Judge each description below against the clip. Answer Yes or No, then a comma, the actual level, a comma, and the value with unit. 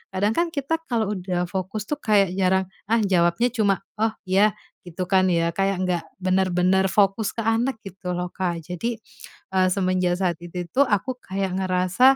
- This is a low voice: No, high, 190 Hz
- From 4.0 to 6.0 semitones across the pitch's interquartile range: No, average, 2.9 semitones